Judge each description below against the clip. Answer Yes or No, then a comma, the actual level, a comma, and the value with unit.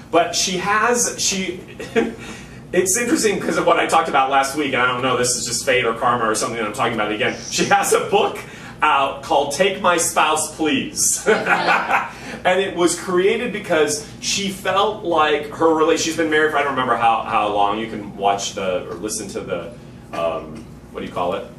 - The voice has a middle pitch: Yes, medium, 160 Hz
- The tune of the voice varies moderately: No, wide, 7.1 semitones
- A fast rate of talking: Yes, fast, 210 wpm